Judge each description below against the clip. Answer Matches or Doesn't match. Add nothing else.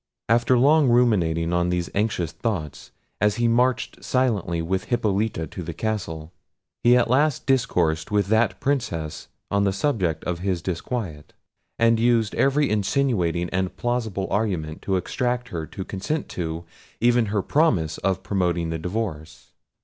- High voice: Doesn't match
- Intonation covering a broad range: Matches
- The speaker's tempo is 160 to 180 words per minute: Doesn't match